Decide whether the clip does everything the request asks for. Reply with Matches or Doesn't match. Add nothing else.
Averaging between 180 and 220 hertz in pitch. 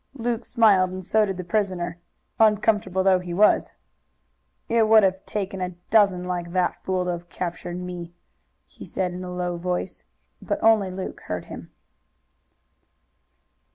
Matches